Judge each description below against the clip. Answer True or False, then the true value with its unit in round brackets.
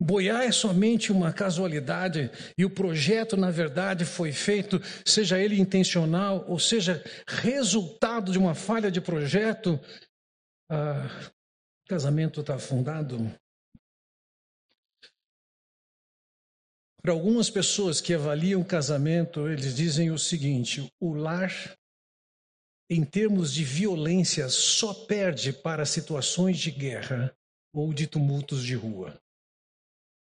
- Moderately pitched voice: True (170 Hz)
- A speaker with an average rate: False (110 wpm)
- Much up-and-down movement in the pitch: False (4.5 semitones)